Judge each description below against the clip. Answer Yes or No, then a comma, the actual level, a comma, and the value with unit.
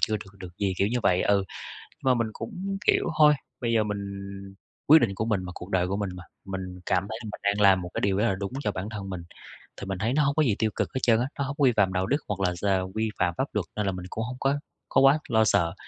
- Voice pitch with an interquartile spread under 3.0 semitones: No, average, 4.1 semitones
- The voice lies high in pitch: No, low, 105 Hz